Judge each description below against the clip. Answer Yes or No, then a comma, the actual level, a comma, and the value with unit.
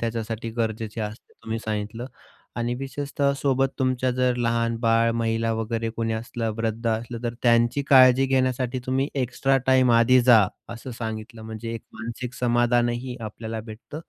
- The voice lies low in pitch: Yes, low, 115 Hz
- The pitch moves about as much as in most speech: No, narrow, 2.1 semitones